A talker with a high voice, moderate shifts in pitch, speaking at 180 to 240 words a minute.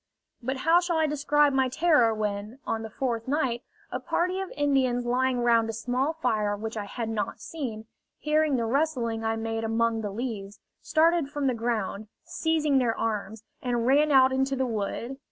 Yes: high, 245 Hz; average, 4.4 semitones; average, 185 wpm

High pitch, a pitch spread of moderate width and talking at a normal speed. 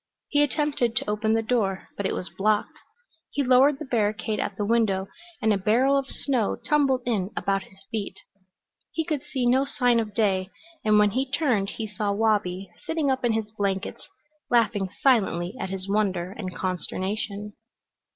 Yes: high, 215 Hz; average, 4.3 semitones; average, 175 wpm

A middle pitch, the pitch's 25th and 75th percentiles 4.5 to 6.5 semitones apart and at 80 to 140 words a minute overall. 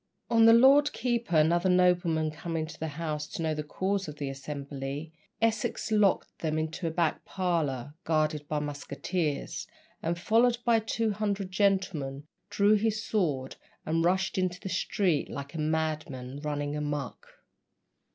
No: medium, 165 Hz; average, 4.8 semitones; average, 160 wpm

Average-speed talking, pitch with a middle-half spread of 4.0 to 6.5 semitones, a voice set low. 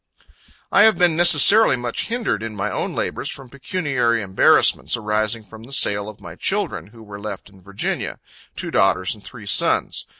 Yes: average, 175 wpm; average, 5.1 semitones; low, 110 Hz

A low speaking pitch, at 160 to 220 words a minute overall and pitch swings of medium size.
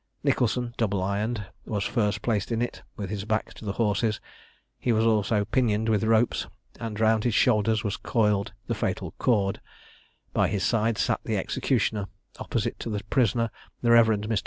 No: low, 110 Hz; average, 175 wpm; narrow, 1.9 semitones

